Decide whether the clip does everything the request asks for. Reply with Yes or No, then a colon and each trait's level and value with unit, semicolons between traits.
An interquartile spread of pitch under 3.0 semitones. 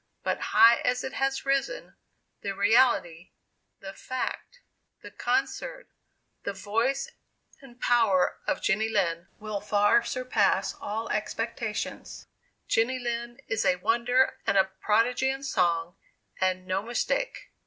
No: average, 4.7 semitones